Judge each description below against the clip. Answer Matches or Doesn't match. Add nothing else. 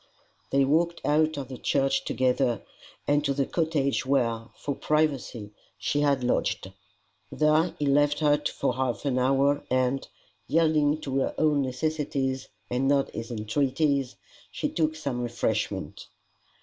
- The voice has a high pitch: Doesn't match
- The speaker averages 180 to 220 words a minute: Doesn't match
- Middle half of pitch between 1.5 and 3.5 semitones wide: Matches